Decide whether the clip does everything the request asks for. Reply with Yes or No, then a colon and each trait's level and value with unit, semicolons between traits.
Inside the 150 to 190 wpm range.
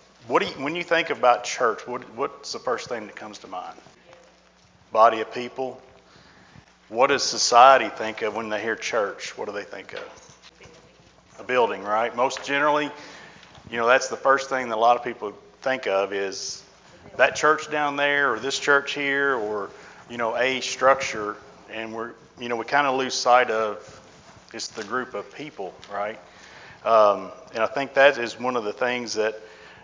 Yes: average, 185 wpm